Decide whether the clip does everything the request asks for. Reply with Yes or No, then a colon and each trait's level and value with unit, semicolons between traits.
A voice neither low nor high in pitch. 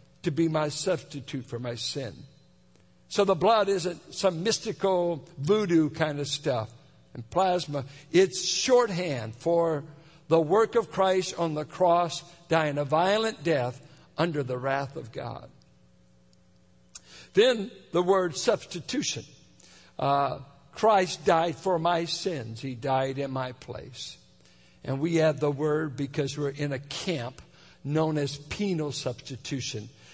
Yes: medium, 150 Hz